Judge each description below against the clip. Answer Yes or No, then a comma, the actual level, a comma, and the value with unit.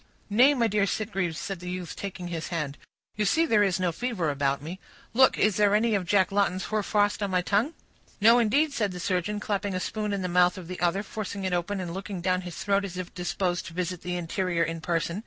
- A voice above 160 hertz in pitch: Yes, high, 190 Hz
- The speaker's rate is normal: No, fast, 235 wpm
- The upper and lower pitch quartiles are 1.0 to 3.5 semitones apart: Yes, average, 2.8 semitones